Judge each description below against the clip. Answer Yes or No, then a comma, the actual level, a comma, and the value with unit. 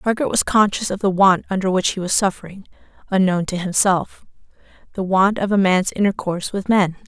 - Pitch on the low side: No, high, 190 Hz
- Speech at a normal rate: Yes, average, 185 wpm